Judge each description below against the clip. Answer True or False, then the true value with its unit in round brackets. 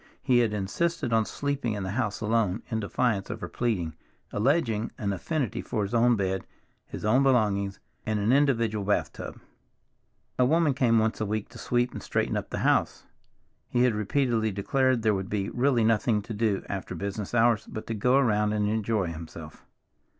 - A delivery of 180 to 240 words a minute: True (185 wpm)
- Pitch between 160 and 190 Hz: False (110 Hz)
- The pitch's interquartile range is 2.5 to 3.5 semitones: True (3.1 semitones)